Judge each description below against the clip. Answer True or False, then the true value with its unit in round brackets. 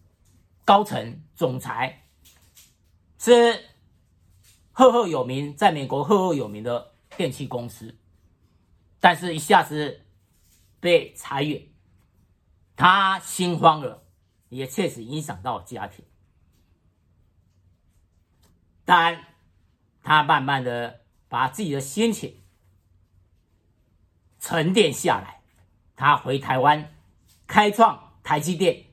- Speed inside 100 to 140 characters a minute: True (135 characters per minute)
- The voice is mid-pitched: False (100 Hz)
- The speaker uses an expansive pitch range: True (9.0 semitones)